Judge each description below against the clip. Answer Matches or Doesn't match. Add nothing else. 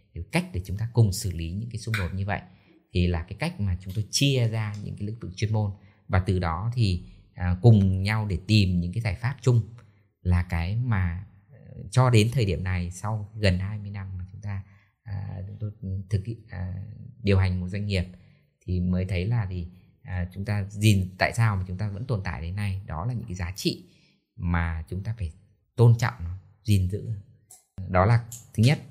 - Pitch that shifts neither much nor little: Matches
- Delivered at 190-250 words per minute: Matches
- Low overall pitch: Matches